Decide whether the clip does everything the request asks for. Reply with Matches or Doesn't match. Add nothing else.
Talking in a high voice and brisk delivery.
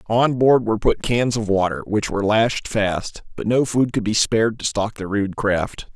Doesn't match